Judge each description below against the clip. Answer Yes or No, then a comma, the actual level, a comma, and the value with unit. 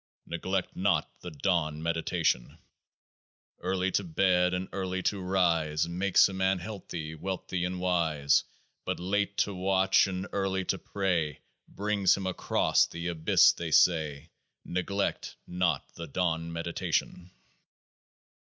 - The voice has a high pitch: No, very low, 90 Hz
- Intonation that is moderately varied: No, narrow, 2.3 semitones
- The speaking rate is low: Yes, slow, 130 wpm